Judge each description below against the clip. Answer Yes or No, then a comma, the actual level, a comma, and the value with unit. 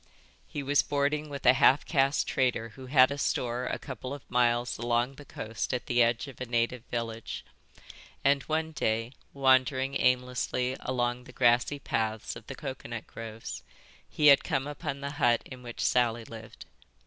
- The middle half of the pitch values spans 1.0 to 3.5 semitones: Yes, average, 2.7 semitones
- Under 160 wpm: No, average, 170 wpm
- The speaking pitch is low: Yes, low, 125 Hz